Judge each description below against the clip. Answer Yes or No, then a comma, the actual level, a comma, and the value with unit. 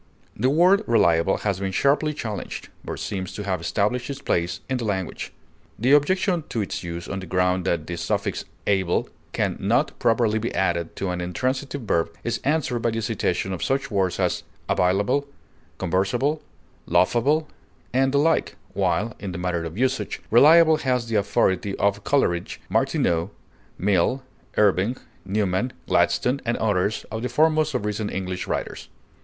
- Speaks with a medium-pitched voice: No, low, 105 Hz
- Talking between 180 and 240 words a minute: No, average, 165 wpm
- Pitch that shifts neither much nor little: No, wide, 6.0 semitones